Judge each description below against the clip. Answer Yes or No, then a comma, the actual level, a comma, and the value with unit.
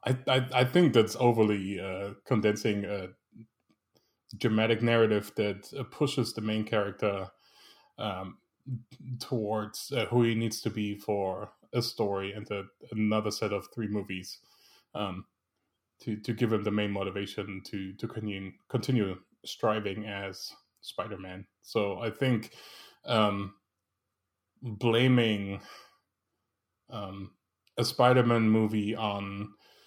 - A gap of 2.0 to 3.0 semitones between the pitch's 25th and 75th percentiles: Yes, narrow, 2.5 semitones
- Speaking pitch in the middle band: No, low, 105 Hz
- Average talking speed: No, slow, 120 wpm